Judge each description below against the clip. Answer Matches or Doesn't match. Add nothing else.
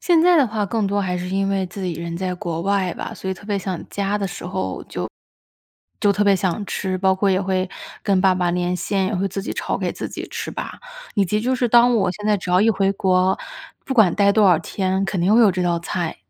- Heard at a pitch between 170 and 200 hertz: Matches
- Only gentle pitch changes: Matches